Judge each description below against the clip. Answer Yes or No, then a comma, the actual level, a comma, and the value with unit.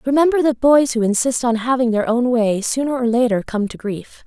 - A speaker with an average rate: No, fast, 225 wpm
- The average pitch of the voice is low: No, high, 245 Hz